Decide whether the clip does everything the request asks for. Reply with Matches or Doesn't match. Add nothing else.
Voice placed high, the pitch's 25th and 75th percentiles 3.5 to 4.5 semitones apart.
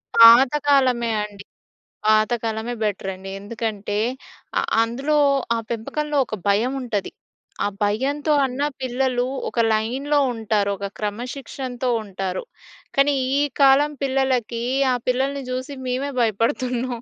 Matches